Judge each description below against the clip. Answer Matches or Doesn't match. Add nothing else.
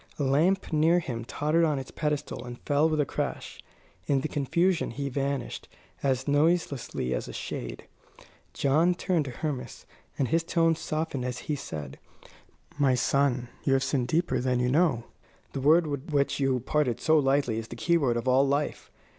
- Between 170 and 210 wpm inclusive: Matches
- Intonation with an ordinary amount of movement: Matches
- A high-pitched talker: Doesn't match